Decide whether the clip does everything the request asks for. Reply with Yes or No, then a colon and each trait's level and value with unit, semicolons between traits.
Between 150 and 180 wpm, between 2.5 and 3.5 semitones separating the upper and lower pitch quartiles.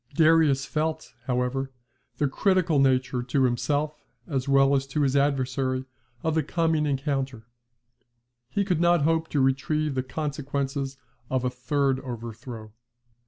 No: slow, 135 wpm; average, 2.8 semitones